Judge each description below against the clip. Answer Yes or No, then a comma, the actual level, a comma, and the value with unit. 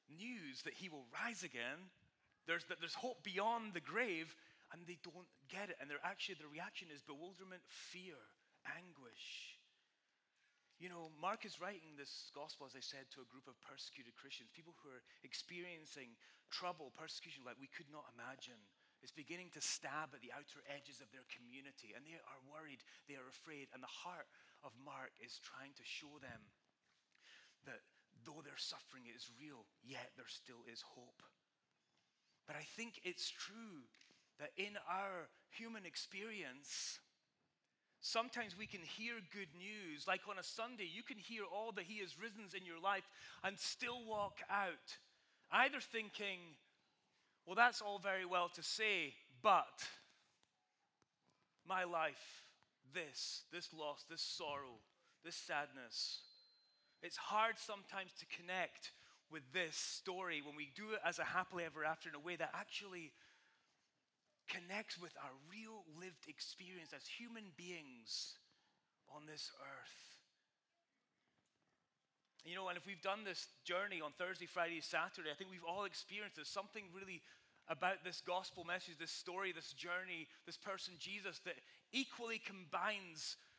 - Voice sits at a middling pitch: Yes, medium, 180 Hz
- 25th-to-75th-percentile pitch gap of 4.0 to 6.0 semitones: Yes, average, 5.0 semitones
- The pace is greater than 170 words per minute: No, average, 155 wpm